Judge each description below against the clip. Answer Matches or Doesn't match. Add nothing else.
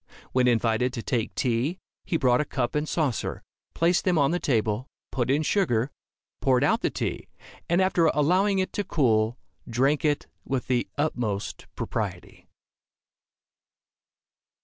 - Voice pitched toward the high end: Doesn't match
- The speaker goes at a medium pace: Matches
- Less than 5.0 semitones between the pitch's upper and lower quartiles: Doesn't match